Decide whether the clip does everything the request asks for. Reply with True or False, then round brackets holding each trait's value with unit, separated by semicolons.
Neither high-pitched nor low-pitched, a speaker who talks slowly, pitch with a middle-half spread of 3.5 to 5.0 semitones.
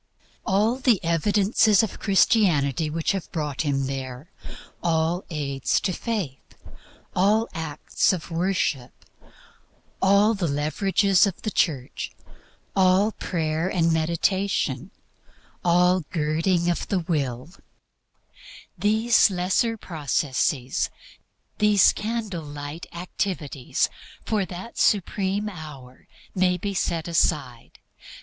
True (175 Hz; 100 wpm; 4.7 semitones)